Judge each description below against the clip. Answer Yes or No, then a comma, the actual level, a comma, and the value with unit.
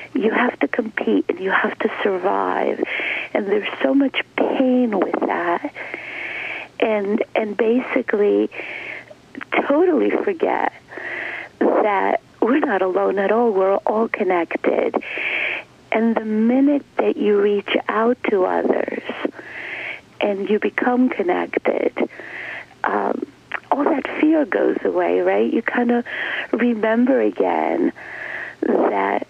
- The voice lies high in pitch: Yes, high, 240 Hz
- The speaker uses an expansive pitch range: Yes, wide, 6.5 semitones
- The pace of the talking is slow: Yes, slow, 115 wpm